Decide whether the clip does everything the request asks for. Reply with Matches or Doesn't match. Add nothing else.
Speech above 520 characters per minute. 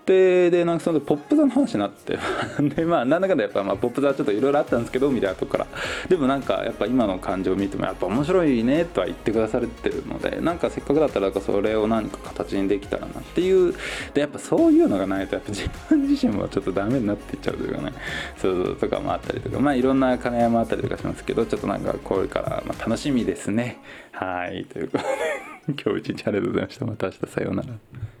Matches